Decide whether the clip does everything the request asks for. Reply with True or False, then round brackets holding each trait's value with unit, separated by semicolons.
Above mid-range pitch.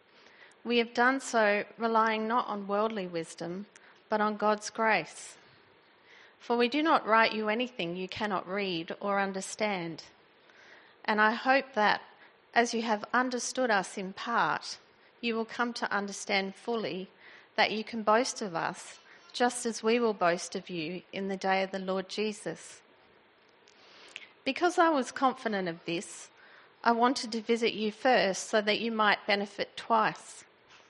True (215 Hz)